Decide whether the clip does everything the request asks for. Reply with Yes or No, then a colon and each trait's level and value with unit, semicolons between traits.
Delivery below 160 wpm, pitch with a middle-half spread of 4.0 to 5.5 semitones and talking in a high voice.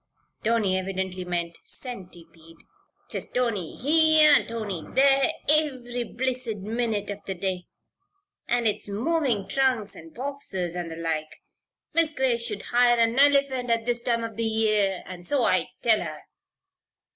Yes: average, 145 wpm; average, 5.2 semitones; high, 225 Hz